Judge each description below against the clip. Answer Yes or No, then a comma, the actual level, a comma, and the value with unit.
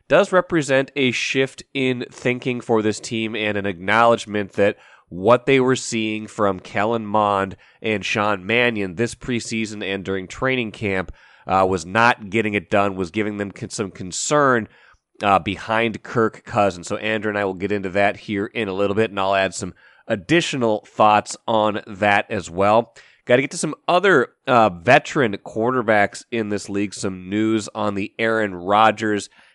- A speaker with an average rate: Yes, average, 175 wpm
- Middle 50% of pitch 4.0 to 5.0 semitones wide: No, narrow, 2.5 semitones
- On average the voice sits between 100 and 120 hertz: Yes, low, 110 Hz